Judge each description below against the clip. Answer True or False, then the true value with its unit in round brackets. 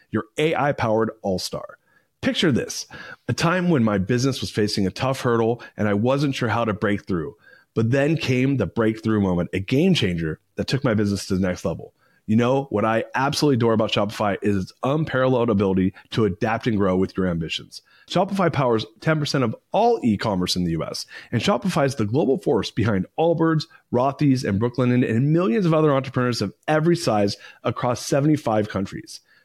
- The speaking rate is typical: True (190 wpm)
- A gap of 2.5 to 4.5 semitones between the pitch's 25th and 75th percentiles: False (5.3 semitones)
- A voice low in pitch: True (115 Hz)